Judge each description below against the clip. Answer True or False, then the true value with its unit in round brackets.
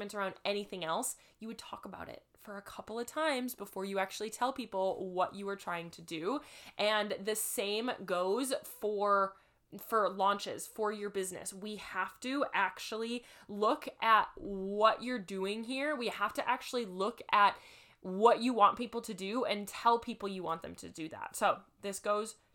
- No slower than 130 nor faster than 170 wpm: False (180 wpm)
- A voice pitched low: False (210 Hz)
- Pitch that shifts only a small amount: False (3.3 semitones)